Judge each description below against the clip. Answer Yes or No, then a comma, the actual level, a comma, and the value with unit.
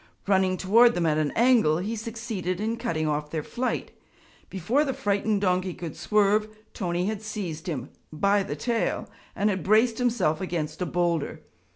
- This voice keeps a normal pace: Yes, average, 170 wpm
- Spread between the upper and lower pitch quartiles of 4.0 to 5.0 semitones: Yes, average, 4.7 semitones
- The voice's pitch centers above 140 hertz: Yes, high, 190 Hz